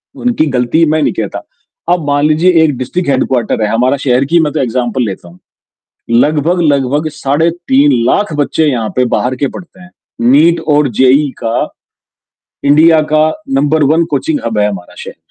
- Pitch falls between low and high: Yes, medium, 145 Hz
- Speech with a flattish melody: No, average, 4.1 semitones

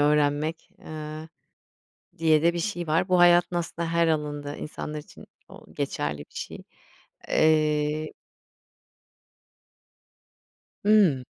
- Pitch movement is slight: Yes, narrow, 2.1 semitones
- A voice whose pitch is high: No, medium, 155 Hz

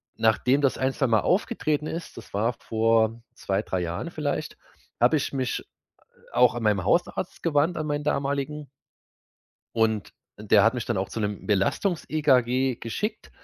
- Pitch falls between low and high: No, low, 125 Hz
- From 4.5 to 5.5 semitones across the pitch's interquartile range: Yes, average, 4.9 semitones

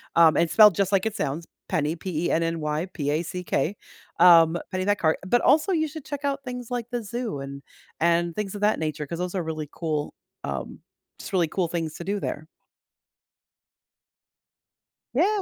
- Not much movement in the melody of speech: No, average, 4.9 semitones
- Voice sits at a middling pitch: Yes, medium, 175 Hz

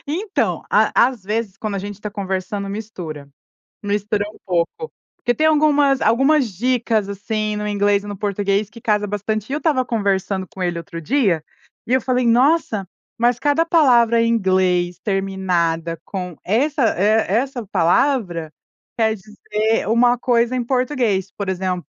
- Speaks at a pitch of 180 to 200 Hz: No, high, 210 Hz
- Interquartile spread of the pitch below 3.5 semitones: No, average, 4.2 semitones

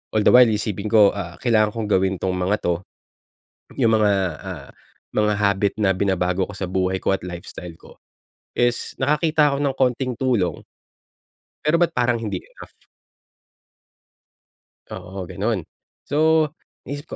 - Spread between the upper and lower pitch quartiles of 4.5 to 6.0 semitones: Yes, average, 5.3 semitones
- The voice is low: Yes, low, 105 Hz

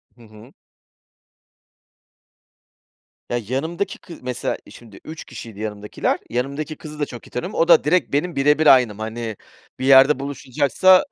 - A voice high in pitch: No, low, 135 Hz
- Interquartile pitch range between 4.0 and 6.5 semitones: Yes, average, 4.6 semitones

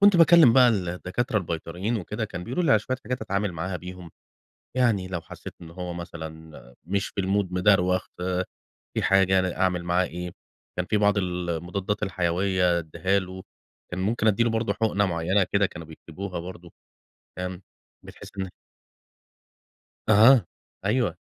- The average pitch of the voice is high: No, very low, 95 Hz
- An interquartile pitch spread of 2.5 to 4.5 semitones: Yes, average, 2.9 semitones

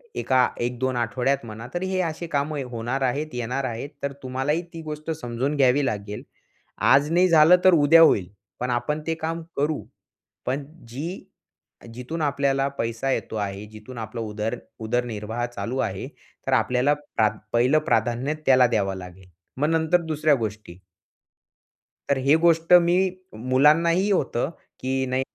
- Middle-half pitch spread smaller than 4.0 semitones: No, average, 4.6 semitones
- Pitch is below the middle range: Yes, low, 130 Hz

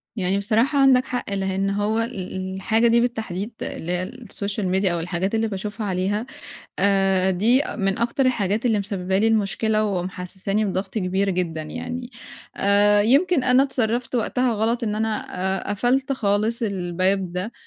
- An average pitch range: Yes, average, 3.5 semitones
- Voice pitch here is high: Yes, high, 205 Hz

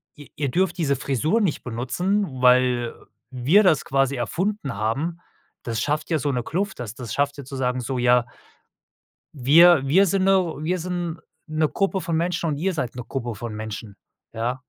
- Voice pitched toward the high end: No, medium, 140 Hz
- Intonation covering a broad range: Yes, wide, 5.8 semitones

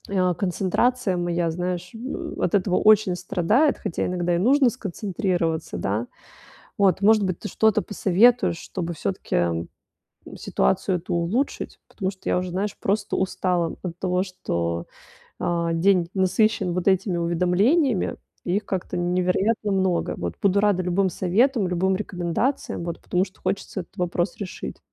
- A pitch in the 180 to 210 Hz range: Yes, medium, 185 Hz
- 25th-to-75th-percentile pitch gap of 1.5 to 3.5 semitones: Yes, average, 2.7 semitones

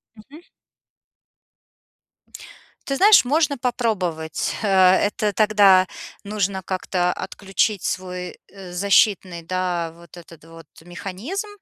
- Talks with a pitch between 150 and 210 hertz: Yes, high, 190 Hz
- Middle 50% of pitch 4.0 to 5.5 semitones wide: No, average, 3.3 semitones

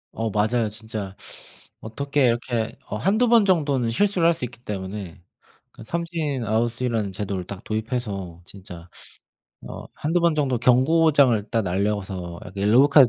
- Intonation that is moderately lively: No, wide, 5.7 semitones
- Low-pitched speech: Yes, low, 115 Hz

